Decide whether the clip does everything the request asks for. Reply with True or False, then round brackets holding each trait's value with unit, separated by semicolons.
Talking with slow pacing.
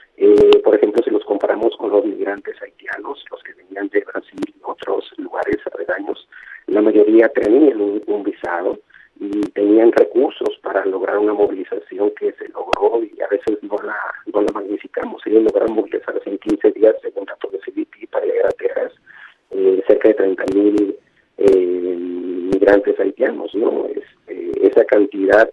False (160 wpm)